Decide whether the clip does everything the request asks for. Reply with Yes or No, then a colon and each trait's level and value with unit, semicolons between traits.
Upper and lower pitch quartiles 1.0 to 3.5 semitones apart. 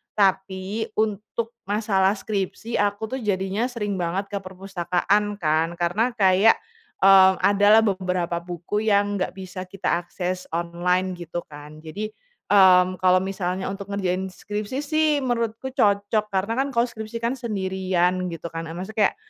Yes: narrow, 2.5 semitones